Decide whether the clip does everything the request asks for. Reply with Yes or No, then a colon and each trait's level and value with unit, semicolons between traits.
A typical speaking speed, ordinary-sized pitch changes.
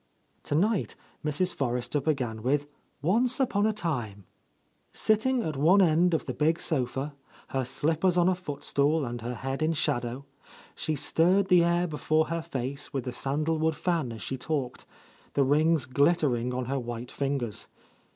Yes: average, 165 wpm; average, 4.7 semitones